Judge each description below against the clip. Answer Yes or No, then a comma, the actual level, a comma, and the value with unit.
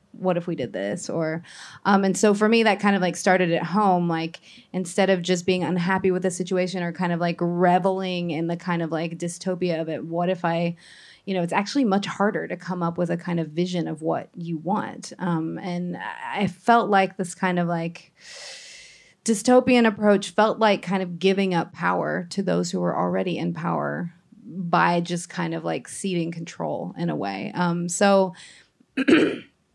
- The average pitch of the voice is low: No, medium, 180 Hz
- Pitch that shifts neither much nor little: No, narrow, 2.3 semitones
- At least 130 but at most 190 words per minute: No, average, 200 wpm